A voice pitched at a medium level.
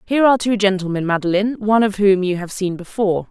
No: high, 200 Hz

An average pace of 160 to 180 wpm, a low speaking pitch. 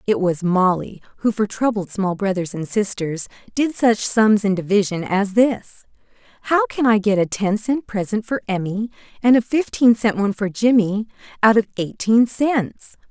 No: average, 175 wpm; high, 210 Hz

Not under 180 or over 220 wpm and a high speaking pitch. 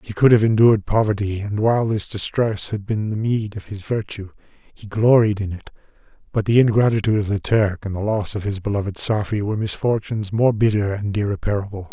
No: average, 195 wpm; low, 105 Hz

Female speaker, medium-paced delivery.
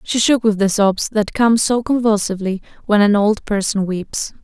Yes: female; average, 190 wpm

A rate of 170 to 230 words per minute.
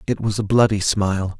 Yes: fast, 215 wpm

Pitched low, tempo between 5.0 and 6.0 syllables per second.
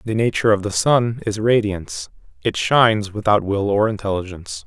Yes: low, 105 Hz; 5.5 syllables/s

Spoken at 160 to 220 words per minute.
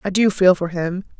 No: fast, 250 wpm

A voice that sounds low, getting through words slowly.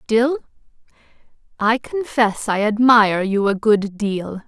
No: high, 220 Hz; slow, 120 wpm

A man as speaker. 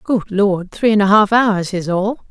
No: female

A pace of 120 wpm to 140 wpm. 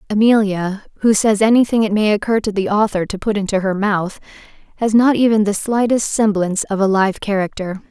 No: average, 190 wpm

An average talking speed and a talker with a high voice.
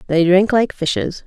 No: average, 190 wpm; medium, 180 Hz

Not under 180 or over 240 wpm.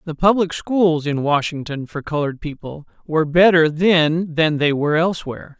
No: average, 160 wpm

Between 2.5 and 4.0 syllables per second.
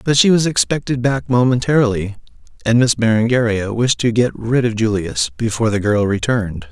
No: 5.5 syllables/s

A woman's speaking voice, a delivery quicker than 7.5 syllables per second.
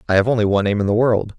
No: male; 8.3 syllables/s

